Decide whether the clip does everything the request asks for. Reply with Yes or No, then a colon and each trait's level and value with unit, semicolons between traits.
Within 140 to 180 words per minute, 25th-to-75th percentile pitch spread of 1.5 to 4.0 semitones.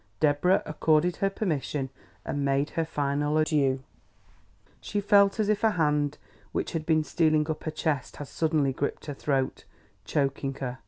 Yes: average, 160 wpm; average, 2.7 semitones